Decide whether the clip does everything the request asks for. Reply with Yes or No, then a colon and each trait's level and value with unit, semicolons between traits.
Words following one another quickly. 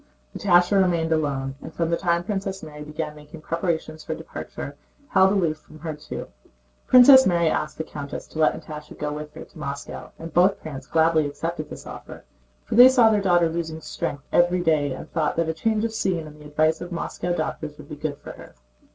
Yes: fast, 210 wpm